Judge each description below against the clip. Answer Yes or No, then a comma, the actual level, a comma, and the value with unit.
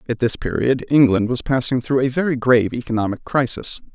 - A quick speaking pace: No, average, 180 wpm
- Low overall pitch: Yes, low, 125 Hz